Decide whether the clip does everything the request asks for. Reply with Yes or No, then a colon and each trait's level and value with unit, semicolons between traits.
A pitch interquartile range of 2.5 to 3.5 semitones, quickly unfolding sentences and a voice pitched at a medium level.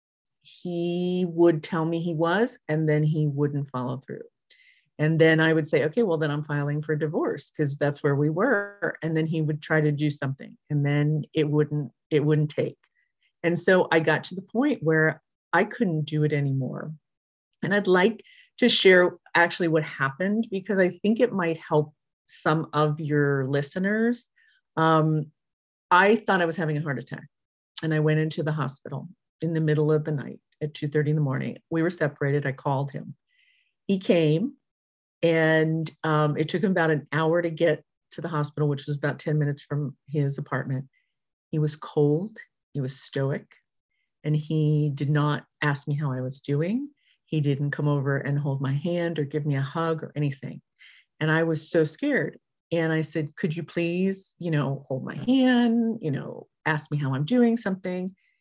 No: average, 2.8 semitones; average, 190 wpm; medium, 155 Hz